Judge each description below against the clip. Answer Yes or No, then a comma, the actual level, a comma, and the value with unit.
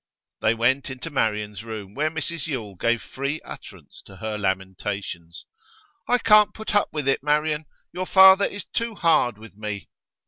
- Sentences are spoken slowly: No, average, 165 wpm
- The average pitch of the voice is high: No, low, 130 Hz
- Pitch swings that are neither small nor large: No, wide, 7.6 semitones